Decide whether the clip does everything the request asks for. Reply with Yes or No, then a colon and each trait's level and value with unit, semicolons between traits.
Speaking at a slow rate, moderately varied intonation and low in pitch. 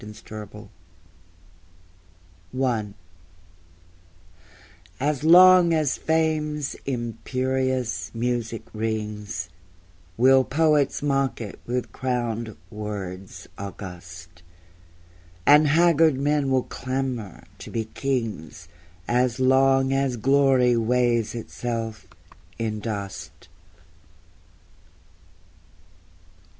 Yes: slow, 75 wpm; average, 4.1 semitones; low, 125 Hz